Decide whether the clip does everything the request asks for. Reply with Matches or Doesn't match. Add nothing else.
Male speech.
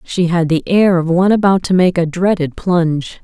Doesn't match